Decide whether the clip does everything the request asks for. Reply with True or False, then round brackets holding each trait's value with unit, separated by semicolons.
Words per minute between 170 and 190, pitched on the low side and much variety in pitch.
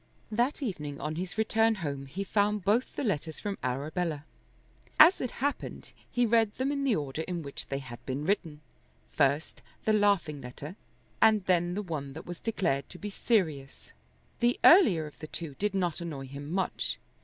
False (180 wpm; 175 Hz; 6.3 semitones)